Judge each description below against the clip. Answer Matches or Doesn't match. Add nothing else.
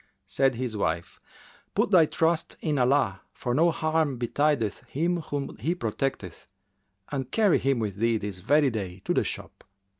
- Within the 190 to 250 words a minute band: Doesn't match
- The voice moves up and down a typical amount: Doesn't match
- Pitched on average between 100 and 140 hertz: Matches